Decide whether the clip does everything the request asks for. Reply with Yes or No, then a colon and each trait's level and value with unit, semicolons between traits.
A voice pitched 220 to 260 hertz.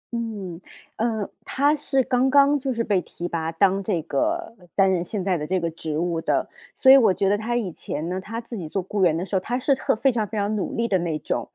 No: high, 205 Hz